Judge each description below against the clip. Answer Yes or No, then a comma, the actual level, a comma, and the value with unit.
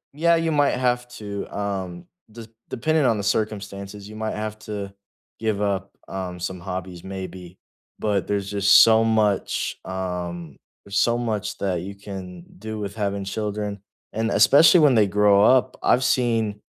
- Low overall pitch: Yes, low, 105 Hz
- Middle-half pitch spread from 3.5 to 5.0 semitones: No, narrow, 2.5 semitones